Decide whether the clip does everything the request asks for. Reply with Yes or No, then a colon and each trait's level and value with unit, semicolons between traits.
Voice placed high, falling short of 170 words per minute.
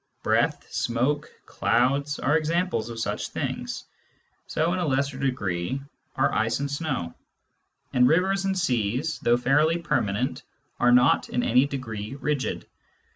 No: low, 135 Hz; average, 140 wpm